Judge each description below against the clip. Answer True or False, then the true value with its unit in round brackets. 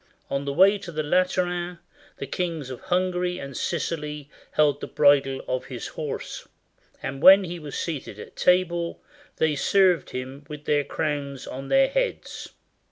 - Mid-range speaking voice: True (155 Hz)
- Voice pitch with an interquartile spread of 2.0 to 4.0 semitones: False (4.4 semitones)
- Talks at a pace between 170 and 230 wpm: False (160 wpm)